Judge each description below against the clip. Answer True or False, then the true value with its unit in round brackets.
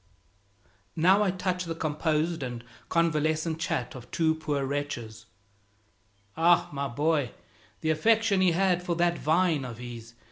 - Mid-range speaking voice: True (160 Hz)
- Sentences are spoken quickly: False (140 wpm)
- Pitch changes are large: False (3.7 semitones)